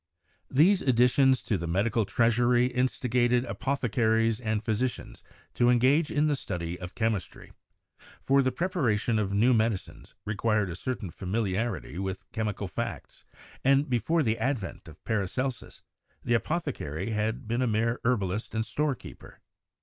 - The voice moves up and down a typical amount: Yes, average, 3.5 semitones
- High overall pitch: No, low, 115 Hz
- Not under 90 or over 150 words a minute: Yes, average, 140 wpm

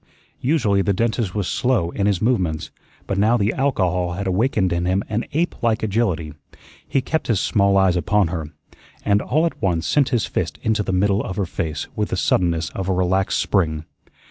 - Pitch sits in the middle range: No, low, 100 Hz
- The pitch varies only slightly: No, average, 3.9 semitones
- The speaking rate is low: No, average, 195 wpm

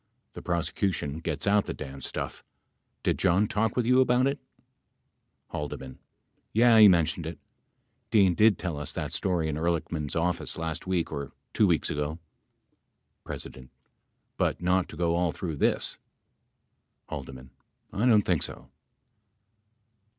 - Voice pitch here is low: Yes, very low, 85 Hz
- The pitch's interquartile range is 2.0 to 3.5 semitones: No, average, 4.5 semitones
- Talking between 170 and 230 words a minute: No, average, 140 wpm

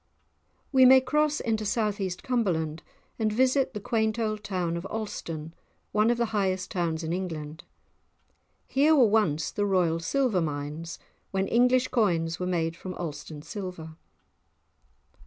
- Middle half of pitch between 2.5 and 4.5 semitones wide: No, wide, 5.5 semitones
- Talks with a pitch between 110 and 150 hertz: No, high, 195 Hz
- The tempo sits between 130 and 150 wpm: Yes, average, 145 wpm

